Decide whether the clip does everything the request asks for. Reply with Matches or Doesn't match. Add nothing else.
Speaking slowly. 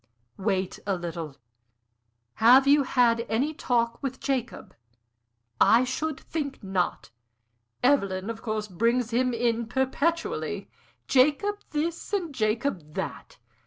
Matches